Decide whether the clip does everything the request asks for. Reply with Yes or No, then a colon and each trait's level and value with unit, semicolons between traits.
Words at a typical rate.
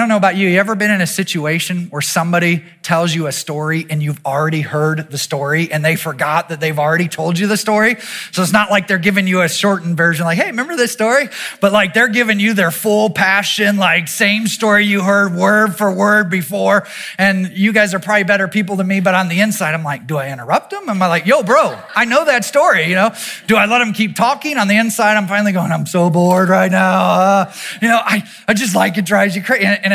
No: fast, 245 wpm